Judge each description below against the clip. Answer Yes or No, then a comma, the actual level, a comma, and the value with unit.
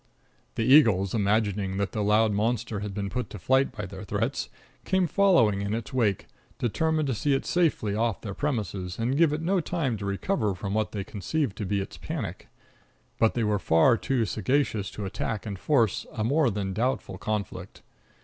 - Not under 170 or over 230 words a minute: Yes, average, 190 wpm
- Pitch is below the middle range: Yes, low, 110 Hz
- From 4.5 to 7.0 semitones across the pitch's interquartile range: Yes, average, 4.8 semitones